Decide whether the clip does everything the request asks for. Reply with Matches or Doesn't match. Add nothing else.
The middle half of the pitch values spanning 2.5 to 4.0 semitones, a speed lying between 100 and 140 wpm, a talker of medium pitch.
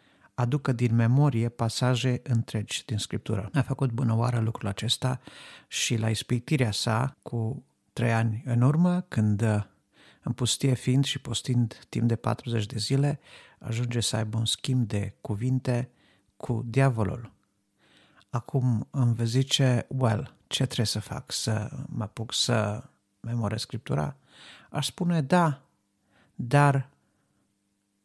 Doesn't match